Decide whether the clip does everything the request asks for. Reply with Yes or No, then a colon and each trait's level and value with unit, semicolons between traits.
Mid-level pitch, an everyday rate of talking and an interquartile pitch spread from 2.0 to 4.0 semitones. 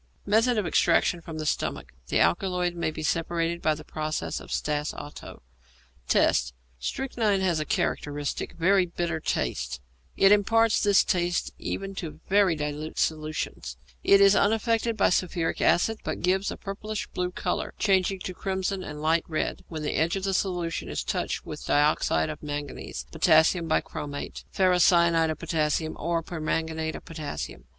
Yes: medium, 170 Hz; average, 160 wpm; average, 3.7 semitones